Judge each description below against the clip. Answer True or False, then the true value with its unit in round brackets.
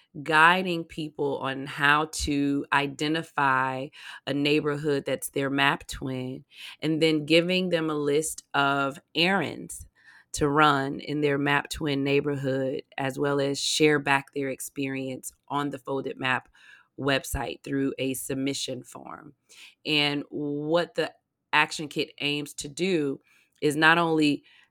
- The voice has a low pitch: False (145 Hz)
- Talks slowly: True (130 wpm)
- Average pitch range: False (1.9 semitones)